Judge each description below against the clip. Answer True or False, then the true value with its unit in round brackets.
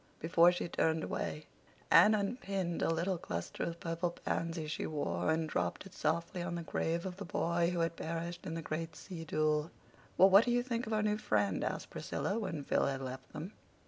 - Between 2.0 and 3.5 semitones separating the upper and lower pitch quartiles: True (3.1 semitones)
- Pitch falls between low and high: True (170 Hz)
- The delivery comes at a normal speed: False (210 wpm)